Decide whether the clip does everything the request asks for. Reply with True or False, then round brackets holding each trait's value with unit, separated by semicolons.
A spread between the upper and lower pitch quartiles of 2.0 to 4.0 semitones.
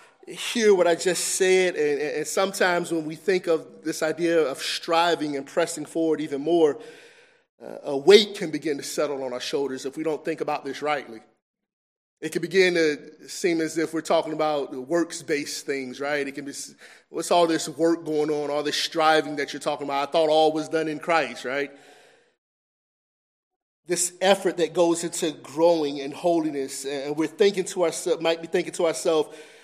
True (2.7 semitones)